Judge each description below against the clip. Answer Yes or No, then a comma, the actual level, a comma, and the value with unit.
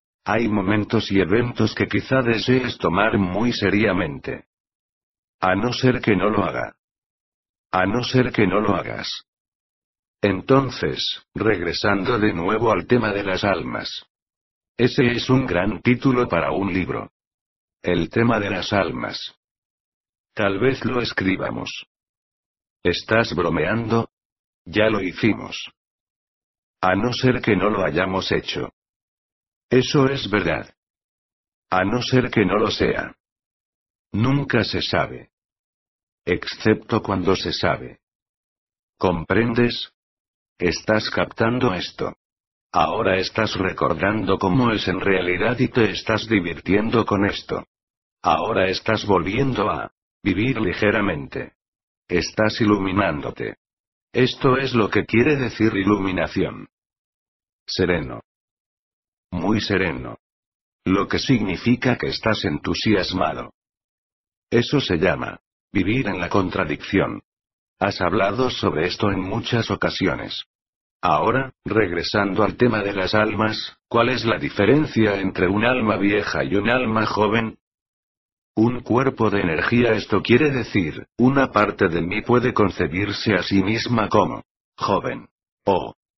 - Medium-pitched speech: No, low, 105 Hz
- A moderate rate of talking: No, slow, 120 wpm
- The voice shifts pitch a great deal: No, average, 3.6 semitones